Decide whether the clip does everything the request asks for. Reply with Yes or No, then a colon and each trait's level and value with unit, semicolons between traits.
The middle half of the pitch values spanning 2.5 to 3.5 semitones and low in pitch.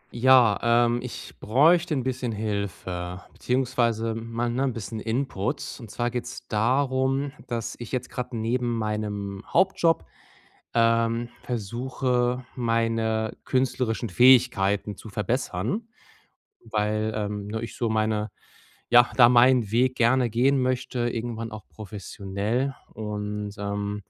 Yes: average, 2.8 semitones; low, 115 Hz